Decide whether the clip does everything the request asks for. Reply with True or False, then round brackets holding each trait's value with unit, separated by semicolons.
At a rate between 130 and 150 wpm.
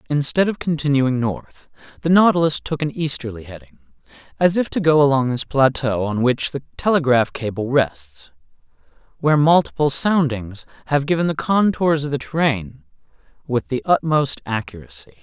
True (145 wpm)